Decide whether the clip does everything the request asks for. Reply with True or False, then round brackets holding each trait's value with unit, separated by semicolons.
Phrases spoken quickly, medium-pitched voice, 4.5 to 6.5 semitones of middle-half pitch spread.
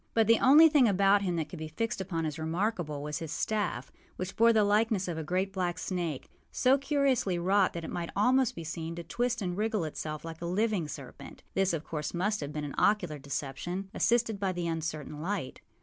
True (215 wpm; 180 Hz; 4.9 semitones)